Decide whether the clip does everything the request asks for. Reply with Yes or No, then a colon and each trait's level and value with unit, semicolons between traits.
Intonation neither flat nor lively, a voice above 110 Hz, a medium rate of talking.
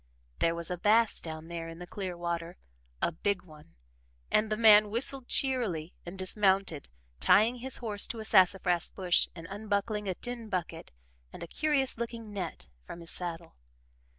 Yes: average, 4.4 semitones; high, 190 Hz; average, 170 wpm